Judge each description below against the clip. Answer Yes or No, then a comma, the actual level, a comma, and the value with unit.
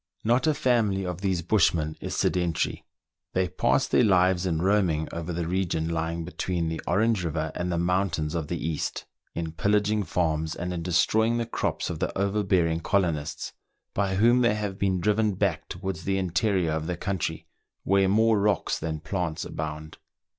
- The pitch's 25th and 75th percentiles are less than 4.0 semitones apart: Yes, average, 3.5 semitones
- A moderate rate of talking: Yes, average, 175 wpm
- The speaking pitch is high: No, very low, 90 Hz